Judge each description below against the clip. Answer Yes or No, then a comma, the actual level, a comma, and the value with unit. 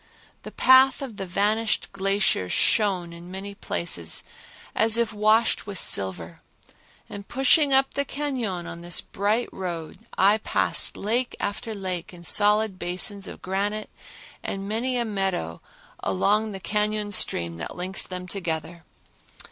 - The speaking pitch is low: No, high, 200 Hz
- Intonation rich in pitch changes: No, average, 3.7 semitones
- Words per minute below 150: Yes, average, 140 wpm